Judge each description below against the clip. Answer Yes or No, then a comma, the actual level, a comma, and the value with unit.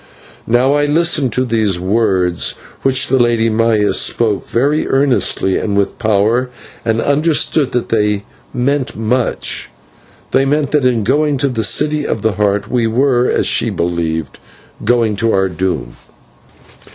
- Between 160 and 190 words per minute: No, average, 150 wpm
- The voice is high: No, low, 115 Hz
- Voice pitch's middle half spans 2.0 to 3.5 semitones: No, average, 4.5 semitones